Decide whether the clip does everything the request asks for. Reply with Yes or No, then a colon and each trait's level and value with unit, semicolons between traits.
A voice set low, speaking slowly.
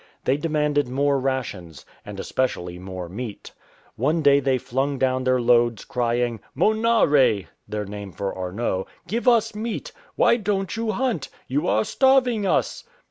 No: low, 130 Hz; average, 150 wpm